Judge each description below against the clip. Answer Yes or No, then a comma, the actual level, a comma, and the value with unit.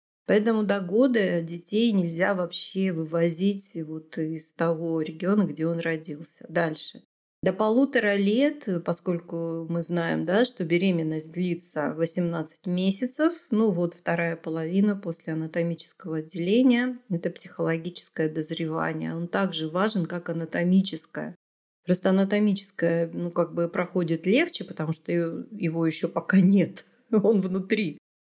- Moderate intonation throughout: Yes, average, 3.1 semitones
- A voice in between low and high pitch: Yes, medium, 175 Hz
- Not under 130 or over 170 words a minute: No, average, 120 wpm